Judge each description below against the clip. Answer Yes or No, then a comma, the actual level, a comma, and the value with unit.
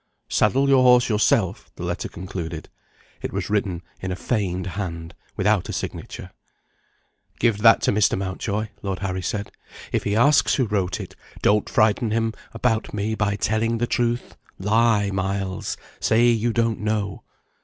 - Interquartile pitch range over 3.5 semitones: No, average, 3.0 semitones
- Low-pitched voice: Yes, low, 105 Hz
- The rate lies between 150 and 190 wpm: Yes, average, 155 wpm